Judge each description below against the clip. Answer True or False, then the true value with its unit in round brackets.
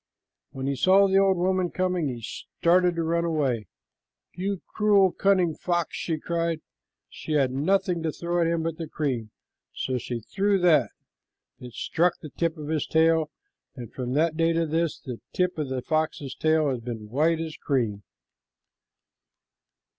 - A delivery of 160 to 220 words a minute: True (170 wpm)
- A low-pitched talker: False (160 Hz)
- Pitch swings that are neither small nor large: True (4.2 semitones)